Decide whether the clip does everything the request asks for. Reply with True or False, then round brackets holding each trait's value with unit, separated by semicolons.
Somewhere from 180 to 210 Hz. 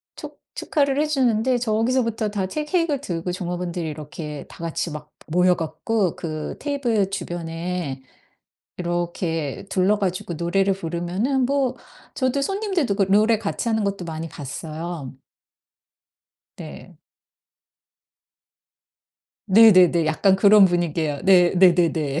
True (185 Hz)